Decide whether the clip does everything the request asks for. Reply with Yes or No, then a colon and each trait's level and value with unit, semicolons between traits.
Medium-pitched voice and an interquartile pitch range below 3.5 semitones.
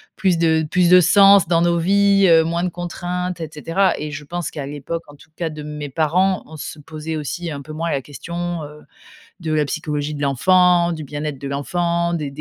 Yes: medium, 165 Hz; average, 2.8 semitones